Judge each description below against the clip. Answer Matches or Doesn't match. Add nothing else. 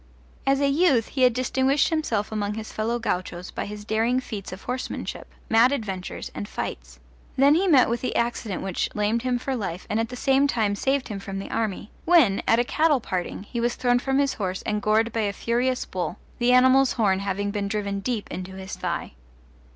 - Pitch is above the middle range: Matches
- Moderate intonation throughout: Matches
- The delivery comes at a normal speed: Doesn't match